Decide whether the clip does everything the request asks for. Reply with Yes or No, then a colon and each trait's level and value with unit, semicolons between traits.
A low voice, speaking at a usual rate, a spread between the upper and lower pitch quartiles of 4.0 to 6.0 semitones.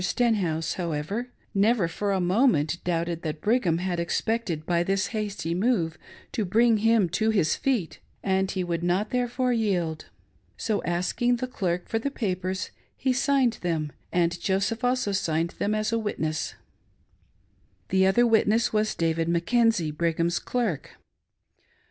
No: high, 190 Hz; average, 150 wpm; average, 5.0 semitones